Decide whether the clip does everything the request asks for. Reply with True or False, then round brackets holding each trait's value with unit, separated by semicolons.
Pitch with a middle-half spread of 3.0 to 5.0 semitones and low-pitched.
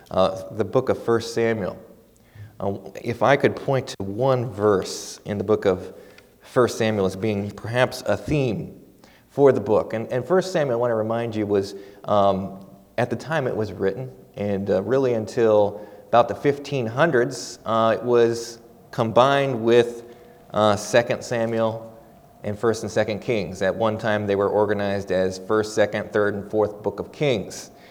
False (2.6 semitones; 110 Hz)